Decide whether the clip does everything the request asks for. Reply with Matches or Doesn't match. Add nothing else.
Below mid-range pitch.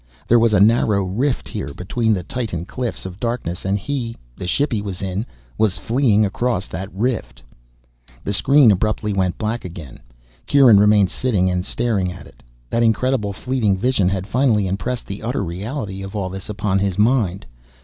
Matches